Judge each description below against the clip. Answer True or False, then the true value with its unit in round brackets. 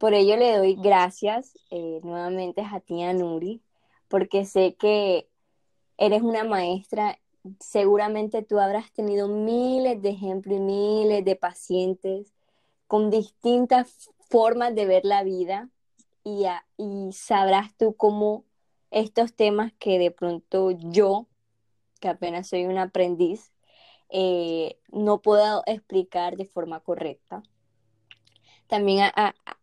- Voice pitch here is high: True (200 Hz)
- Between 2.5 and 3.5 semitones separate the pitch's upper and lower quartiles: True (2.9 semitones)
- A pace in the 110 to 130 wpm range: True (125 wpm)